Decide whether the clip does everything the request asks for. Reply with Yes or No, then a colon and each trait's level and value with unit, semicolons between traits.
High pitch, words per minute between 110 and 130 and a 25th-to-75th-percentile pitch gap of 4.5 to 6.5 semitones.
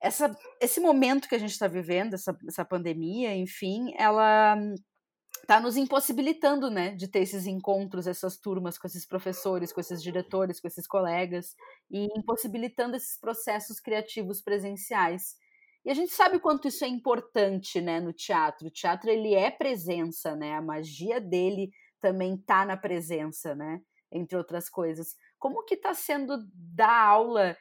No: high, 195 Hz; average, 155 wpm; average, 5.2 semitones